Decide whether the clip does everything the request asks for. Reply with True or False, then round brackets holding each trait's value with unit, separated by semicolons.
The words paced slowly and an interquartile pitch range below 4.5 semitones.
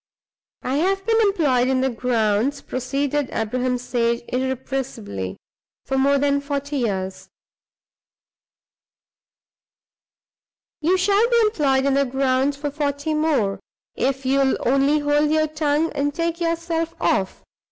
True (125 wpm; 3.2 semitones)